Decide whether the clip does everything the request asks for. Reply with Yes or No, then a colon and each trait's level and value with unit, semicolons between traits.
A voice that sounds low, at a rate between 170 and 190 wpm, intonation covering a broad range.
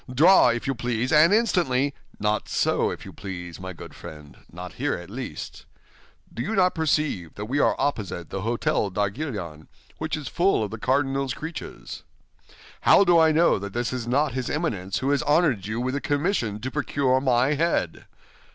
Yes: low, 130 Hz; average, 180 wpm; wide, 6.6 semitones